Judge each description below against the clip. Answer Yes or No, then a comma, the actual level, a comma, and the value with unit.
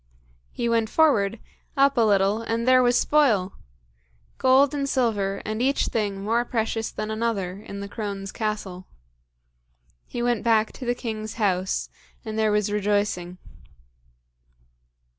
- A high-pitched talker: Yes, high, 220 Hz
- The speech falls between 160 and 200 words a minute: No, average, 140 wpm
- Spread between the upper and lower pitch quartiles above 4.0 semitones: No, average, 3.1 semitones